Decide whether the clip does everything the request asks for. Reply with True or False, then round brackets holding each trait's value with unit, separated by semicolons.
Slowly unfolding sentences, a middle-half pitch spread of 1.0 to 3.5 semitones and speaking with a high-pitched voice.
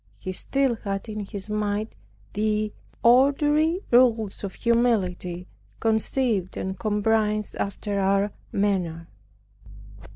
True (100 wpm; 2.9 semitones; 210 Hz)